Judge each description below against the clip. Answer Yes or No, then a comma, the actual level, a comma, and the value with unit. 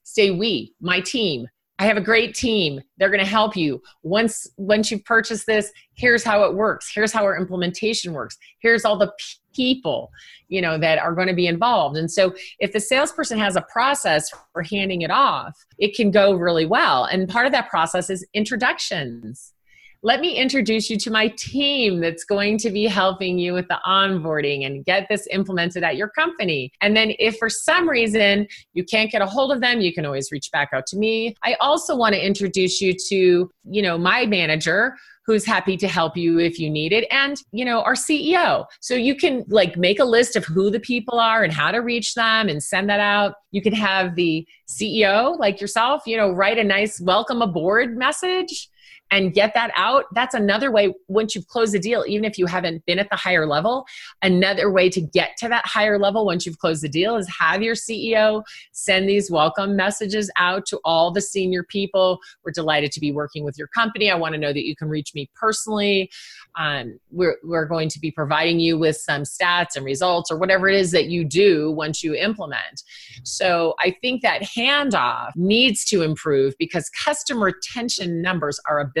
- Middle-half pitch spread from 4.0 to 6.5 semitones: Yes, average, 4.3 semitones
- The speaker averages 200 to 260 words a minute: Yes, fast, 205 wpm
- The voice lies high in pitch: Yes, high, 200 Hz